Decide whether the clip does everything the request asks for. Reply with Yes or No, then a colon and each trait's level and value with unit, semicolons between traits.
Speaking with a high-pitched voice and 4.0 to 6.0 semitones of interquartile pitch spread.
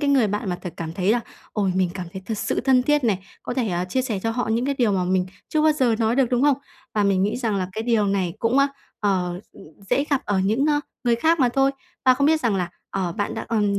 Yes: high, 225 Hz; average, 5.2 semitones